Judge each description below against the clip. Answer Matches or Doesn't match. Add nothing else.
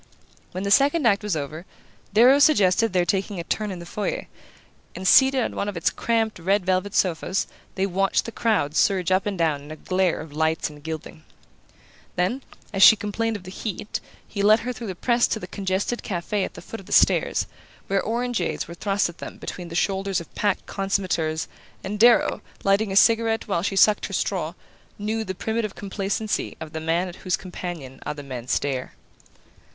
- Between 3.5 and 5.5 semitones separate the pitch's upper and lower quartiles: Matches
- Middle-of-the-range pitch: Doesn't match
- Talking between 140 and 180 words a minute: Doesn't match